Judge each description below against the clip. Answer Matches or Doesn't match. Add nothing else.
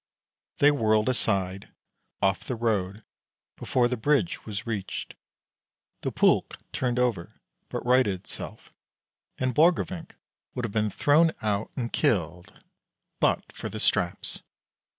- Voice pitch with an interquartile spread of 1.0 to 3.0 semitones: Doesn't match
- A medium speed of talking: Doesn't match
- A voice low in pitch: Matches